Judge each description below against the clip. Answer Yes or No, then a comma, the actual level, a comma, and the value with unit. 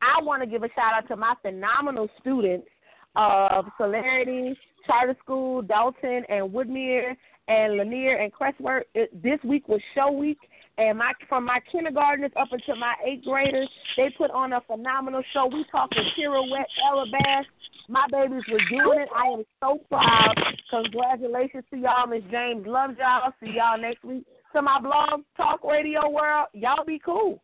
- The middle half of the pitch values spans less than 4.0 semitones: Yes, average, 3.2 semitones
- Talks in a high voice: Yes, very high, 260 Hz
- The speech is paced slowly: No, average, 170 wpm